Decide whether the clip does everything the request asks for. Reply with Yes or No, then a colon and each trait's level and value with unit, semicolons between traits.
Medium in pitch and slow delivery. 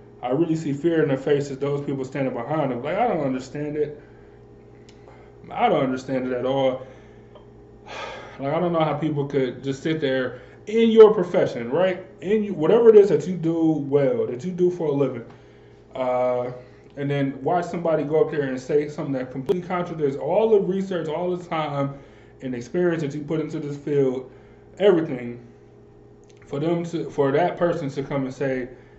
No: medium, 145 Hz; average, 190 wpm